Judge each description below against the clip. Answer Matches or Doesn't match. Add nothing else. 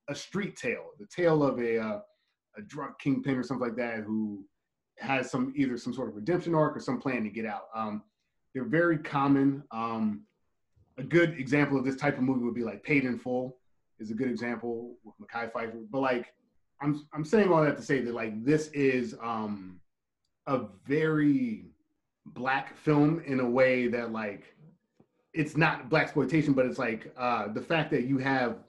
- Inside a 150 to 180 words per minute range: Doesn't match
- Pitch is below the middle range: Matches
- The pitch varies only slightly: Doesn't match